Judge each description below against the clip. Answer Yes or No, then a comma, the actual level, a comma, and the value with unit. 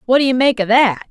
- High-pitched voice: Yes, high, 240 Hz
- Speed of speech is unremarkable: No, fast, 325 wpm